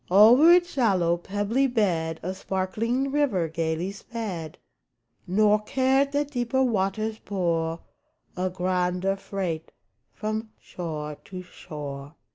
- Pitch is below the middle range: No, high, 195 Hz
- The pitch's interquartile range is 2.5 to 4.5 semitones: No, average, 5.1 semitones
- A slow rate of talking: Yes, slow, 110 wpm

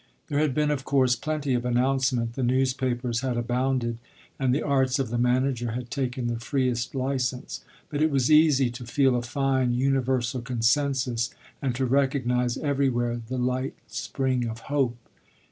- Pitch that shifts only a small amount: Yes, narrow, 2.0 semitones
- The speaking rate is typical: Yes, average, 160 wpm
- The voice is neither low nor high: No, low, 130 Hz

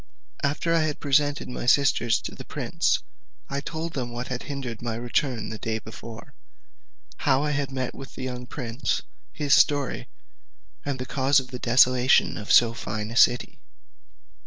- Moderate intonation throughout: Yes, average, 3.0 semitones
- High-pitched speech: No, low, 130 Hz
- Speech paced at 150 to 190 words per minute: Yes, average, 170 wpm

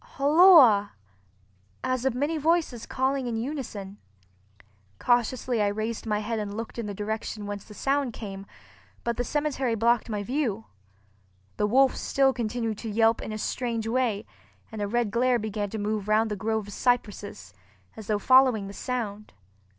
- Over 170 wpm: No, average, 165 wpm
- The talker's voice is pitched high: Yes, high, 225 Hz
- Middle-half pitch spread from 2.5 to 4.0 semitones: Yes, average, 3.4 semitones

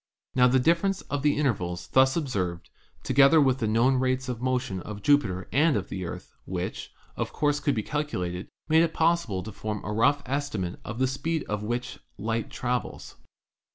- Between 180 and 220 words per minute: Yes, average, 185 wpm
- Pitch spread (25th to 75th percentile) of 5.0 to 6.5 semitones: Yes, wide, 5.4 semitones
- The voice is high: No, low, 125 Hz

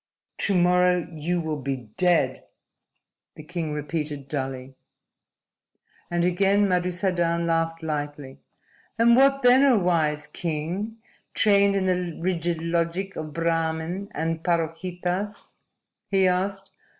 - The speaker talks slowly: Yes, slow, 115 wpm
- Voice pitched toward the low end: No, medium, 170 Hz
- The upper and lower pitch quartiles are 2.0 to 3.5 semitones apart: Yes, average, 2.8 semitones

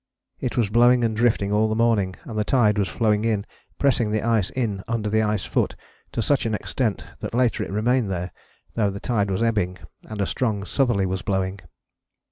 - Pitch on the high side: No, low, 110 Hz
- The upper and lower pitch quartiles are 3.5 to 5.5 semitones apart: No, average, 2.8 semitones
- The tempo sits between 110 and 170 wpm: No, fast, 205 wpm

